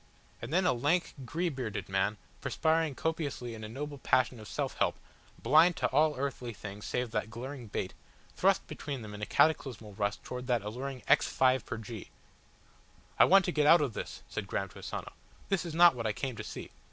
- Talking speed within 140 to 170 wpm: No, fast, 205 wpm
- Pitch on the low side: Yes, low, 125 Hz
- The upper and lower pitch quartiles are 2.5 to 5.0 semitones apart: No, wide, 5.6 semitones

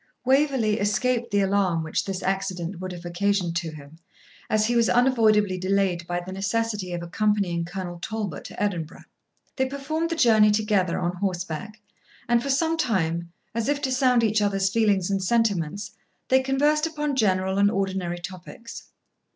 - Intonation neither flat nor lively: Yes, average, 4.5 semitones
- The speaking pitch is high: Yes, high, 200 Hz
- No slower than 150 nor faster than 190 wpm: Yes, average, 165 wpm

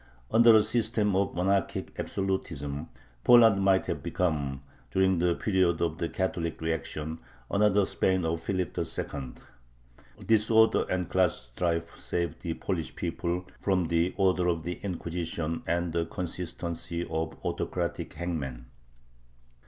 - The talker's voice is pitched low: Yes, very low, 85 Hz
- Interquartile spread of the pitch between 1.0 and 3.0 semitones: Yes, average, 2.7 semitones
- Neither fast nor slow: No, slow, 130 wpm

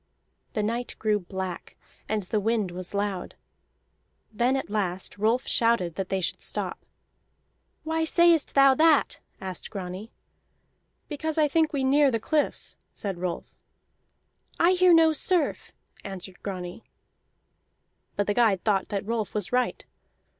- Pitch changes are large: Yes, wide, 6.8 semitones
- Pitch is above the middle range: Yes, high, 220 Hz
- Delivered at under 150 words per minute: Yes, average, 140 wpm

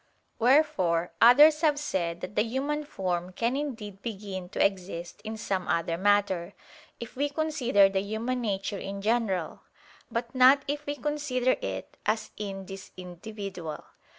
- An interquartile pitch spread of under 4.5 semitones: No, average, 5.2 semitones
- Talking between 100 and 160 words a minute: Yes, average, 150 wpm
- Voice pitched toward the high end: Yes, high, 210 Hz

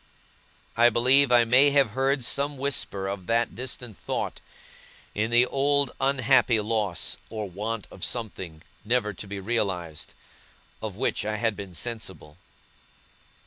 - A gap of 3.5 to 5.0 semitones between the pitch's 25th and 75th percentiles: Yes, average, 4.1 semitones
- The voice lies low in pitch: Yes, low, 115 Hz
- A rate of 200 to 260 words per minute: No, average, 140 wpm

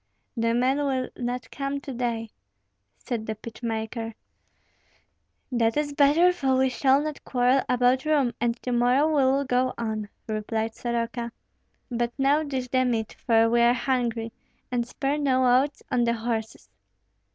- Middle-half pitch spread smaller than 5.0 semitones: Yes, narrow, 2.6 semitones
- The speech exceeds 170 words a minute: No, average, 160 wpm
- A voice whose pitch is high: Yes, high, 245 Hz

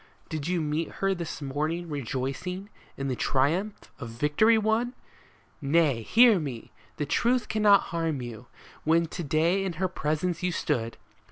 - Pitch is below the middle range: No, medium, 165 Hz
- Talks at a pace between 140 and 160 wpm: Yes, average, 155 wpm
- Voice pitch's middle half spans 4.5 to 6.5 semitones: Yes, average, 5.2 semitones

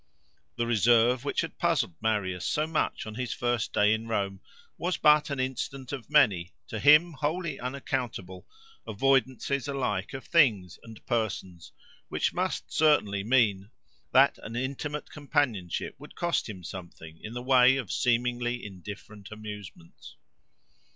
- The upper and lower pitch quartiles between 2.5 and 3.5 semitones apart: No, average, 4.9 semitones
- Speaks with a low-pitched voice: Yes, low, 120 Hz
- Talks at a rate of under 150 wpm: Yes, average, 140 wpm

